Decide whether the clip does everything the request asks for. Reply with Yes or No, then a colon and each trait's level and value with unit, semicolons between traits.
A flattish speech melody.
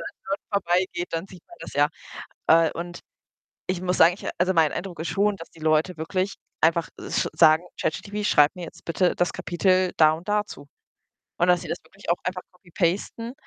Yes: narrow, 2.3 semitones